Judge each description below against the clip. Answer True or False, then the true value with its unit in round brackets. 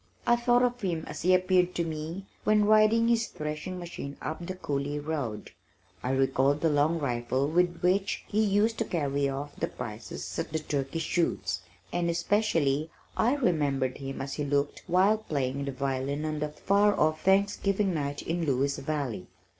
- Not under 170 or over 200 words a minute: True (175 wpm)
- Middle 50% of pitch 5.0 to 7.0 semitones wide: True (5.4 semitones)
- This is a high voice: False (155 Hz)